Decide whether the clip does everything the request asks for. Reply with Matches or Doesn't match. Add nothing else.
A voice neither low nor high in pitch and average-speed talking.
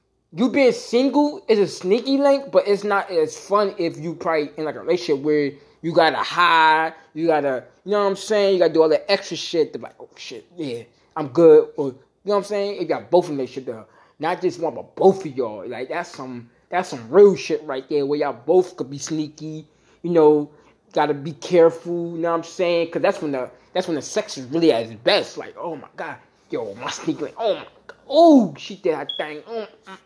Doesn't match